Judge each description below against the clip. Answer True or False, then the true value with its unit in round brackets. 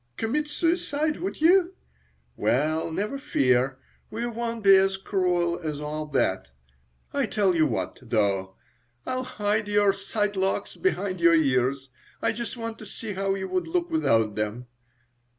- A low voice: False (195 Hz)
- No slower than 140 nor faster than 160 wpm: True (150 wpm)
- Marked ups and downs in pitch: True (8.2 semitones)